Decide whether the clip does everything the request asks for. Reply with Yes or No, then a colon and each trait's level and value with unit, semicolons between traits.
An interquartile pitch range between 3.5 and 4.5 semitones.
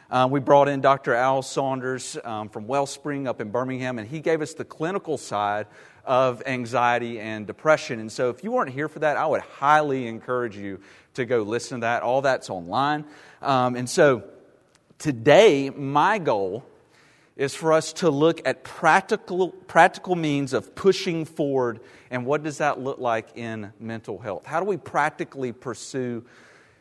Yes: average, 4.1 semitones